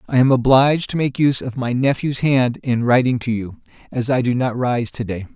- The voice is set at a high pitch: No, low, 125 Hz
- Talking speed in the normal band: No, fast, 235 wpm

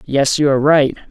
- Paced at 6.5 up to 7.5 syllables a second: No, 5.6 syllables/s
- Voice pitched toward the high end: No, medium, 140 Hz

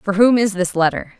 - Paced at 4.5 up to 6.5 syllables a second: Yes, 5.4 syllables/s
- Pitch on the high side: Yes, high, 195 Hz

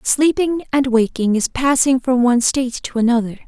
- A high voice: Yes, very high, 250 Hz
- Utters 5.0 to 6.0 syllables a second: Yes, 5.2 syllables/s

